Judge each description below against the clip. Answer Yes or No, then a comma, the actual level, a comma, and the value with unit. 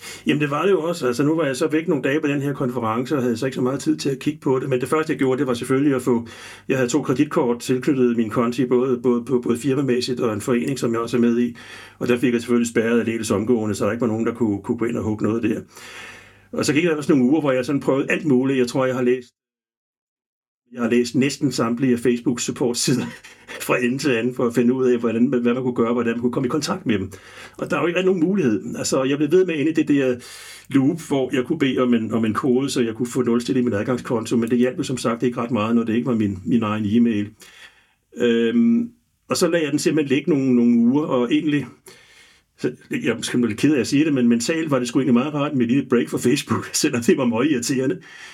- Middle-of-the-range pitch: No, low, 125 Hz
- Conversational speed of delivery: No, fast, 280 wpm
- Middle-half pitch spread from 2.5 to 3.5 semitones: Yes, average, 2.8 semitones